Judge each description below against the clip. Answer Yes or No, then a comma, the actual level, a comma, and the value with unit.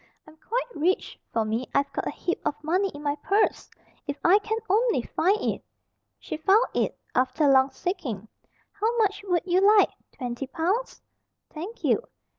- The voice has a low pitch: No, very high, 345 Hz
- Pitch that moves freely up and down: Yes, wide, 6.5 semitones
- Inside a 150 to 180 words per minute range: Yes, average, 170 wpm